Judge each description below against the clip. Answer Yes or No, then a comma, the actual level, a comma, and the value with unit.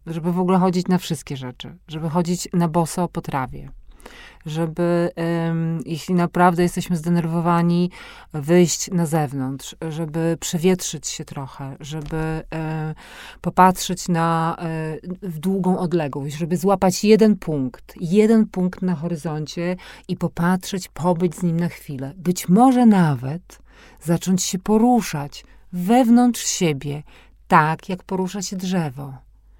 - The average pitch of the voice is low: No, medium, 170 Hz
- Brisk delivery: No, average, 120 wpm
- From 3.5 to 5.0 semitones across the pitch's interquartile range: No, narrow, 2.5 semitones